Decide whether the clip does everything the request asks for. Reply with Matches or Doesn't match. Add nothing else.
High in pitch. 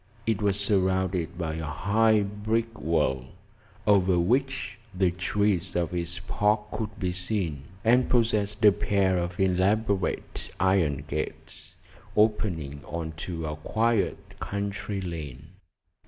Doesn't match